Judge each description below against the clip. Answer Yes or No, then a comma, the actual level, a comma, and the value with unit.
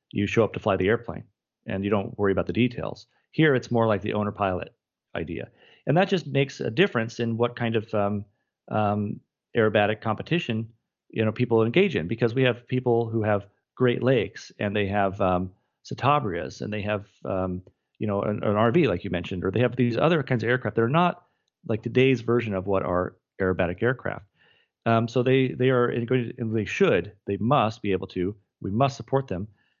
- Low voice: Yes, low, 110 Hz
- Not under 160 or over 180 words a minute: No, fast, 205 wpm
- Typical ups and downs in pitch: Yes, average, 3.5 semitones